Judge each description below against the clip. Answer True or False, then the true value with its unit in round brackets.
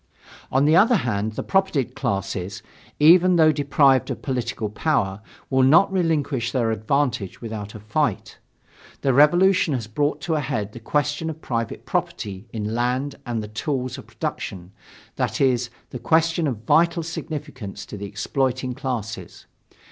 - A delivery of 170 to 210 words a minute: False (155 wpm)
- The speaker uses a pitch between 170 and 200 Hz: False (130 Hz)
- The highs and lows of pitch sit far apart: True (5.7 semitones)